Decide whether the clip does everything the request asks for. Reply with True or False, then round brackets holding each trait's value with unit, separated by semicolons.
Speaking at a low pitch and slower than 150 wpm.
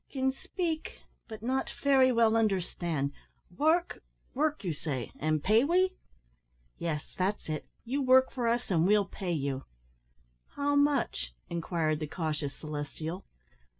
False (205 Hz; 140 wpm)